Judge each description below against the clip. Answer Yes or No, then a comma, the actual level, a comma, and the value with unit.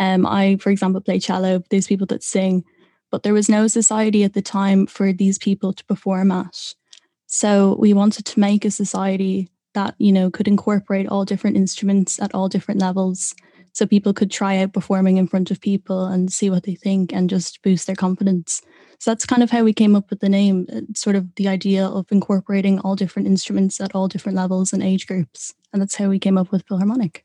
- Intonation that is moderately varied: No, narrow, 1.2 semitones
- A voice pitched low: No, high, 195 Hz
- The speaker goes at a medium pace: No, fast, 215 wpm